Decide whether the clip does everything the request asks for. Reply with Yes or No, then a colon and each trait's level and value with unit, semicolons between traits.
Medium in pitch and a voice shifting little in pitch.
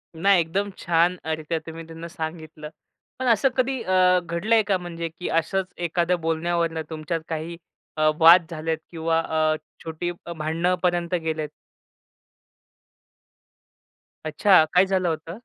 Yes: medium, 170 Hz; narrow, 2.1 semitones